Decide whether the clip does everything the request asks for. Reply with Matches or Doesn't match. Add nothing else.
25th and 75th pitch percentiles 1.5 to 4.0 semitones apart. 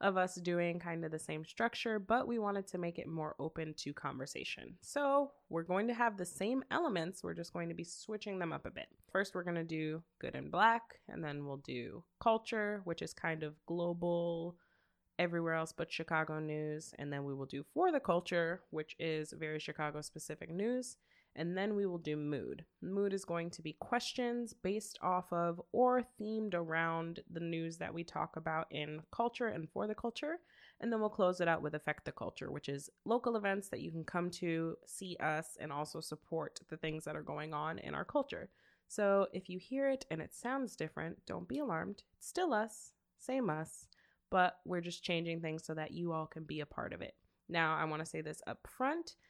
Doesn't match